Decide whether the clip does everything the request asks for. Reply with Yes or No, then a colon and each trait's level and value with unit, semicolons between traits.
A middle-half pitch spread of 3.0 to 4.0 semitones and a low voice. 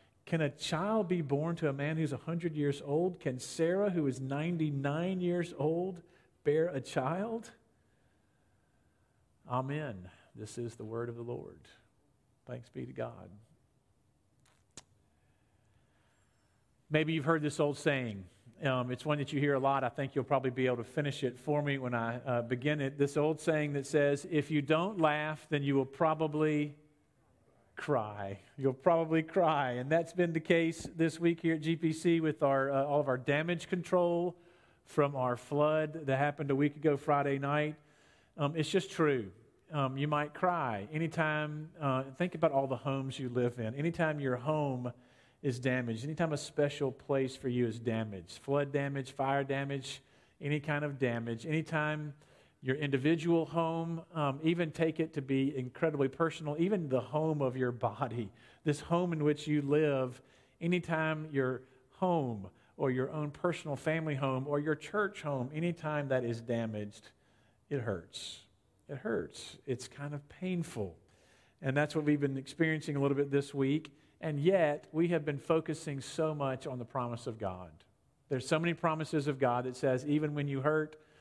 No: average, 3.4 semitones; medium, 145 Hz